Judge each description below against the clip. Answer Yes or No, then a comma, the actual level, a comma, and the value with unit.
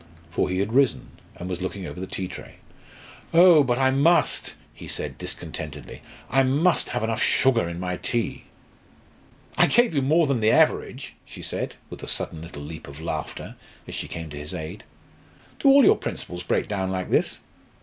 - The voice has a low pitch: Yes, low, 100 Hz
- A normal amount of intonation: No, wide, 7.6 semitones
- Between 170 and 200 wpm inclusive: Yes, average, 190 wpm